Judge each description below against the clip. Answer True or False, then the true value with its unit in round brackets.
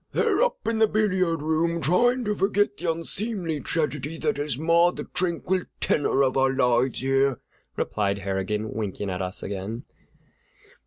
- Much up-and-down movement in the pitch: True (7.5 semitones)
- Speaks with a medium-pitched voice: True (155 Hz)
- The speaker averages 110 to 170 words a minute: True (160 wpm)